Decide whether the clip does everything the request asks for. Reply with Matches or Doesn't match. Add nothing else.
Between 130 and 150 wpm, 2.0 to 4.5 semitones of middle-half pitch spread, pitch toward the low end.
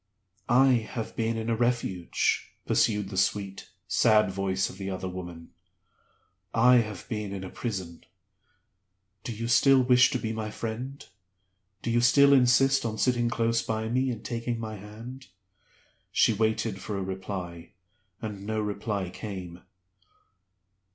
Matches